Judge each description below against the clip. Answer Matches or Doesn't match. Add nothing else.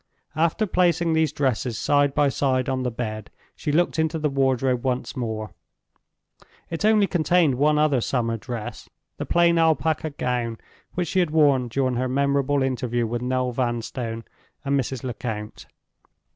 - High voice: Doesn't match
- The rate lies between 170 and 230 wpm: Doesn't match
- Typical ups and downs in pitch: Matches